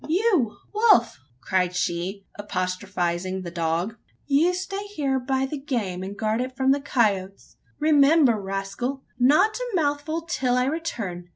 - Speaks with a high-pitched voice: Yes, very high, 250 Hz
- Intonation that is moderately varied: No, wide, 7.8 semitones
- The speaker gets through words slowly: No, average, 145 wpm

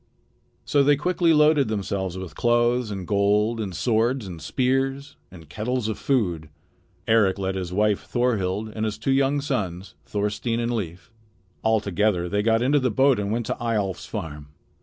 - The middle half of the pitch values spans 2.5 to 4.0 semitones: No, average, 4.5 semitones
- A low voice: Yes, low, 110 Hz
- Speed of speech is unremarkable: Yes, average, 170 wpm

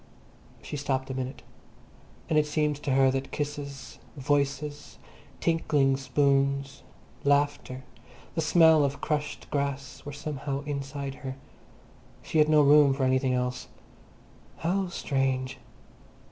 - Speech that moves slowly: Yes, slow, 120 wpm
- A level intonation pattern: Yes, narrow, 1.8 semitones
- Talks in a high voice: No, medium, 140 Hz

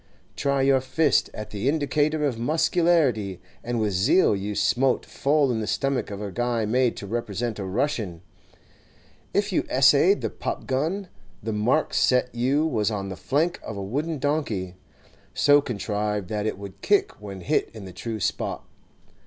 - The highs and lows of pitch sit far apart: Yes, wide, 5.7 semitones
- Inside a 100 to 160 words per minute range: No, average, 170 wpm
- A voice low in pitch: Yes, low, 120 Hz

